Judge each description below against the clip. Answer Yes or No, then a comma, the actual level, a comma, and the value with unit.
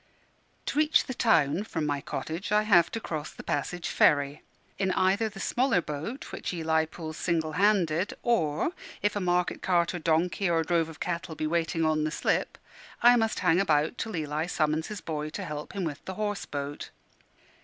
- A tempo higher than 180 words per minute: Yes, average, 190 wpm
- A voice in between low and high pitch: Yes, medium, 170 Hz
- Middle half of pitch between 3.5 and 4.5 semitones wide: Yes, average, 4.2 semitones